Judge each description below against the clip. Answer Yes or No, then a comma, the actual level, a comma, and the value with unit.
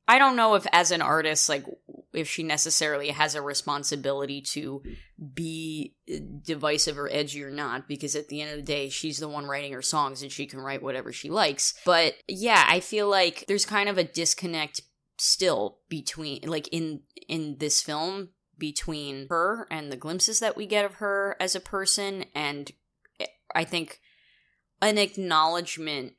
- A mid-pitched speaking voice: Yes, medium, 155 Hz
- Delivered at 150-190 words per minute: Yes, average, 175 wpm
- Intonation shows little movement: No, average, 3.7 semitones